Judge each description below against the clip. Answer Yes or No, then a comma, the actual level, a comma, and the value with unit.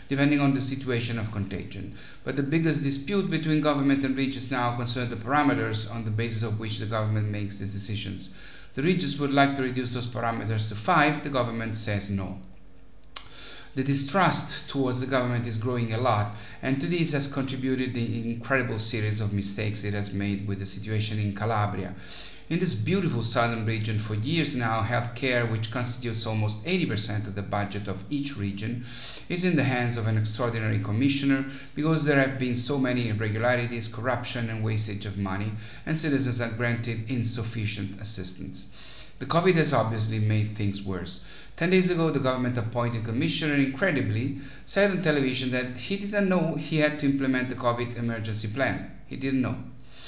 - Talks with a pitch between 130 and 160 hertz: No, low, 120 Hz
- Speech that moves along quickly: No, average, 180 wpm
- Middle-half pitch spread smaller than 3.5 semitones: No, average, 4.3 semitones